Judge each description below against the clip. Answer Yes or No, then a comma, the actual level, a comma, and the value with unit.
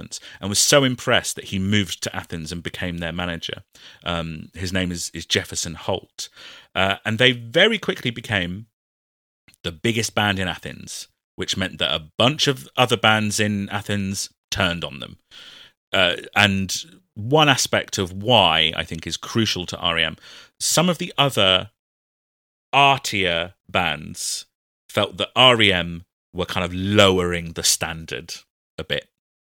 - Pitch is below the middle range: Yes, low, 100 Hz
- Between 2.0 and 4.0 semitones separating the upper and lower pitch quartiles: No, average, 5.0 semitones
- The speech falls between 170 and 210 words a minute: No, average, 150 wpm